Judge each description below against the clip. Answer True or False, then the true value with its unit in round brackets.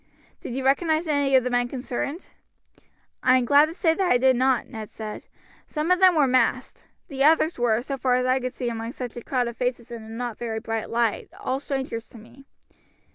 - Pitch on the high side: True (255 Hz)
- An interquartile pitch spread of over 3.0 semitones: False (2.7 semitones)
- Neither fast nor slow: False (220 wpm)